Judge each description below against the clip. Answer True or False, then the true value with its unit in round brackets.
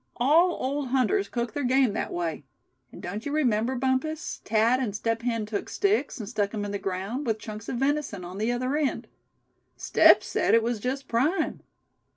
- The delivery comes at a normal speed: True (190 wpm)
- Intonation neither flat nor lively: True (4.3 semitones)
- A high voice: True (240 Hz)